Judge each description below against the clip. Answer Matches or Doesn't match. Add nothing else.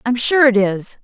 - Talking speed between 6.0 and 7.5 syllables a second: Doesn't match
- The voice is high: Matches